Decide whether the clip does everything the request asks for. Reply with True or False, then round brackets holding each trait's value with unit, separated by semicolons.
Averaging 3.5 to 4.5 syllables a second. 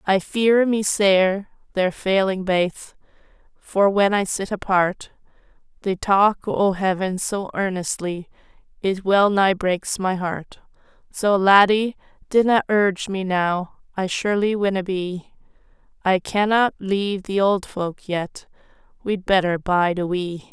True (3.9 syllables/s)